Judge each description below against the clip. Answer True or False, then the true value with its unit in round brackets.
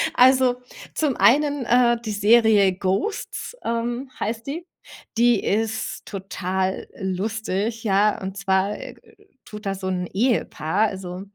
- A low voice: False (215 Hz)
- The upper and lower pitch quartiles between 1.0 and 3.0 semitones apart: False (3.8 semitones)